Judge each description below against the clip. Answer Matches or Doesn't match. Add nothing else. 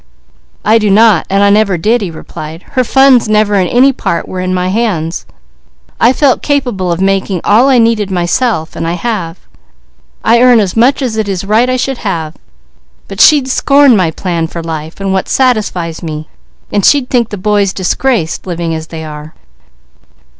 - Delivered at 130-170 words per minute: Doesn't match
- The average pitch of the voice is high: Matches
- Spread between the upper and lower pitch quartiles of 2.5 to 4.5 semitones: Doesn't match